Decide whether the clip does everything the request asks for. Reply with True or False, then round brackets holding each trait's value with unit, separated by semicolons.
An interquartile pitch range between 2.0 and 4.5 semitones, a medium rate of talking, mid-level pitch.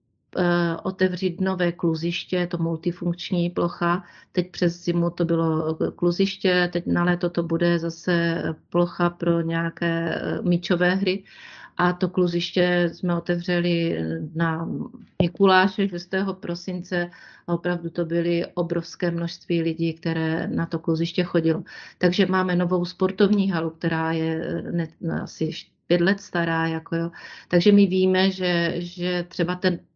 False (1.3 semitones; 130 wpm; 175 Hz)